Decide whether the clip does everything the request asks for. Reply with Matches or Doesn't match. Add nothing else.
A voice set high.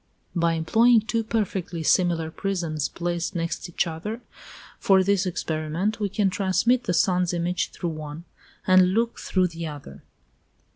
Doesn't match